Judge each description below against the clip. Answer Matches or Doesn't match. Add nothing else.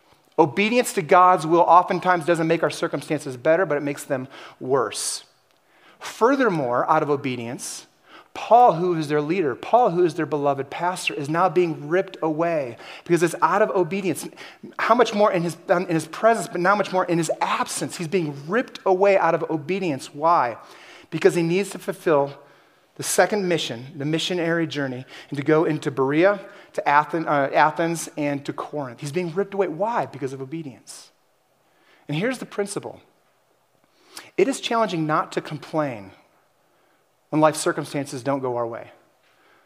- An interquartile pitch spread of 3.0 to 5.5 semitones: Matches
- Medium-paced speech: Matches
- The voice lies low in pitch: Doesn't match